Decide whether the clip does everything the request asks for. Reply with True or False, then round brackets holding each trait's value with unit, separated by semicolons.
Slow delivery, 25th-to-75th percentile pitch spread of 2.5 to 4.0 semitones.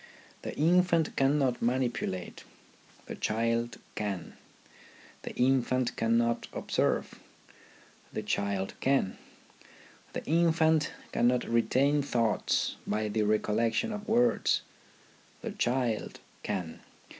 False (100 wpm; 5.3 semitones)